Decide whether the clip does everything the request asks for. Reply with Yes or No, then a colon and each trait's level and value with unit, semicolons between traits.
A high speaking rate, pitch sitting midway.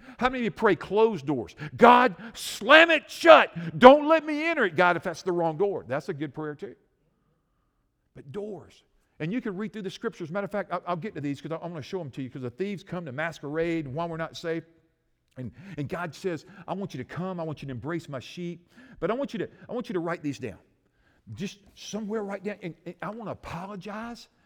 Yes: fast, 250 wpm; medium, 175 Hz